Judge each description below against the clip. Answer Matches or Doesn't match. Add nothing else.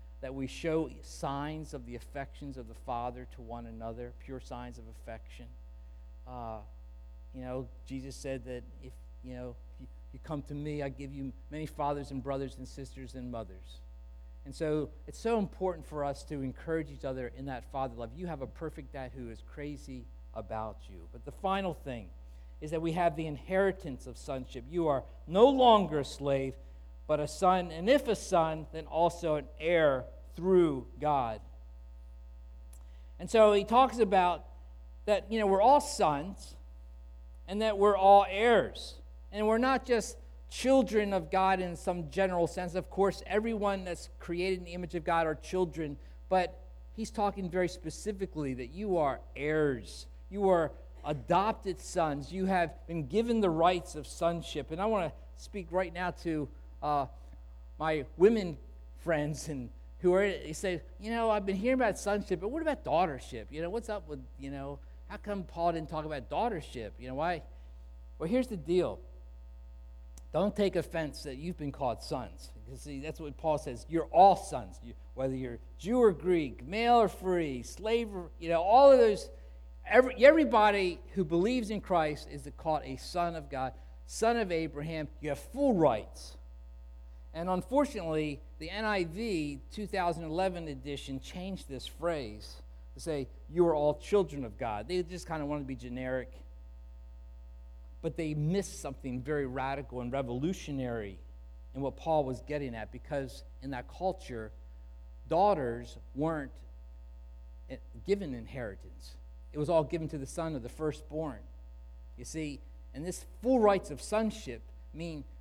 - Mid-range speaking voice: Matches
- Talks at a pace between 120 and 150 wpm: Doesn't match